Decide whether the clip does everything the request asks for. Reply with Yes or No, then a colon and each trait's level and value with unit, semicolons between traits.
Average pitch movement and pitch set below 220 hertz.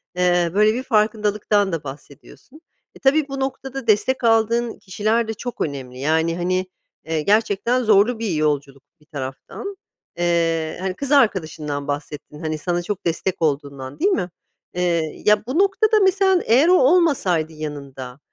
No: wide, 7.5 semitones; high, 190 Hz